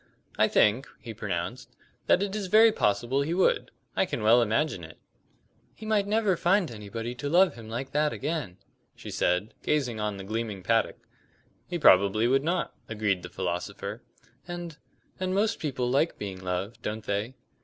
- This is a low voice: Yes, low, 120 Hz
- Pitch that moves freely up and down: Yes, wide, 8.3 semitones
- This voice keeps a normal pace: Yes, average, 170 wpm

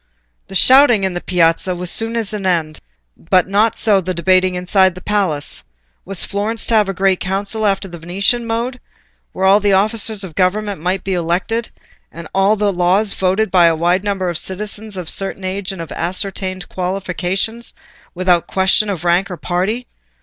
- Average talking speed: Yes, average, 185 wpm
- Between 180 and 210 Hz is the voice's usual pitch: Yes, high, 190 Hz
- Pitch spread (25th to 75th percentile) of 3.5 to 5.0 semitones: No, narrow, 2.5 semitones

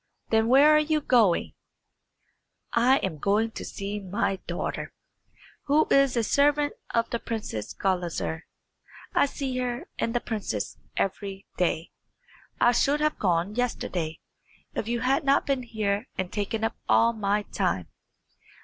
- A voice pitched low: No, high, 225 Hz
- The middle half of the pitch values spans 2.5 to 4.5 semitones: No, average, 5.0 semitones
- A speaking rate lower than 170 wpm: Yes, average, 145 wpm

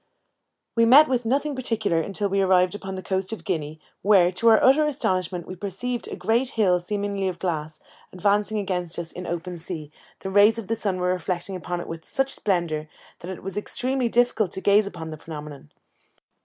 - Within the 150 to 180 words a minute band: No, average, 200 wpm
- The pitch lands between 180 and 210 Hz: Yes, high, 190 Hz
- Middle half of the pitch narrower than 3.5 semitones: No, average, 4.0 semitones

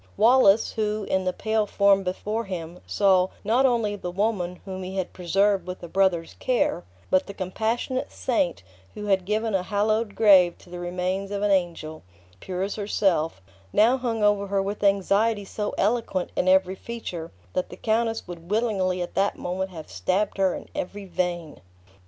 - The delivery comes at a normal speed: Yes, average, 175 wpm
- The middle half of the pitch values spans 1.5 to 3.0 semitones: Yes, average, 2.7 semitones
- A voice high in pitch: Yes, high, 195 Hz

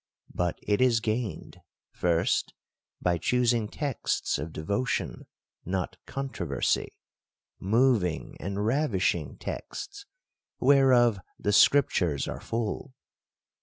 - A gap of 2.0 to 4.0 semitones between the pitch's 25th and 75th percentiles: No, wide, 5.6 semitones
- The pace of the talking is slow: Yes, slow, 100 wpm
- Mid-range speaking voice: No, low, 110 Hz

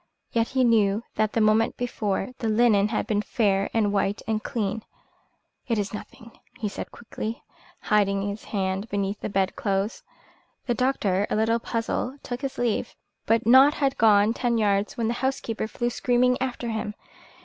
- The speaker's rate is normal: Yes, average, 170 wpm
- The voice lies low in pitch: No, high, 220 Hz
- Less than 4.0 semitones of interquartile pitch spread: Yes, average, 2.7 semitones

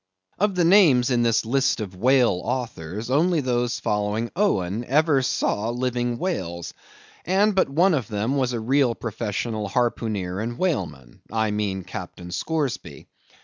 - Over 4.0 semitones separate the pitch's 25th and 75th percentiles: Yes, average, 4.9 semitones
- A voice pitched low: Yes, low, 120 Hz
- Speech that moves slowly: No, average, 145 wpm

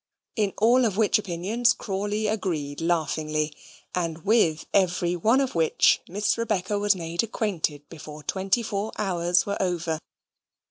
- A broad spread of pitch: No, average, 4.3 semitones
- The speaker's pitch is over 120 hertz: Yes, high, 190 Hz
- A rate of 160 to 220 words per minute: No, average, 140 wpm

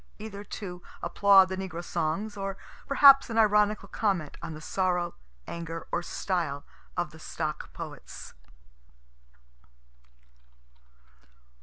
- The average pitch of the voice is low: No, high, 190 Hz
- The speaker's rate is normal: No, slow, 110 wpm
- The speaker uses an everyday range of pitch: Yes, average, 3.4 semitones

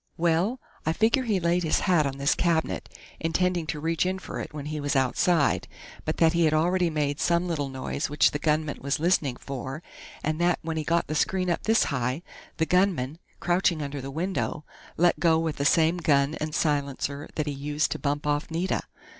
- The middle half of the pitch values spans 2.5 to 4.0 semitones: Yes, average, 3.1 semitones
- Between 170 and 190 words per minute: No, fast, 205 wpm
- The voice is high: No, medium, 160 Hz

